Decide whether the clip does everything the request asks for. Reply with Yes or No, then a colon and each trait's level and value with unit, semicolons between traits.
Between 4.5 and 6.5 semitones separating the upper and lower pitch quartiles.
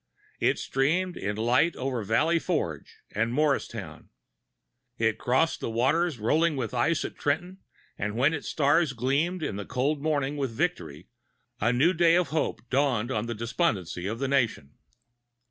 Yes: wide, 5.5 semitones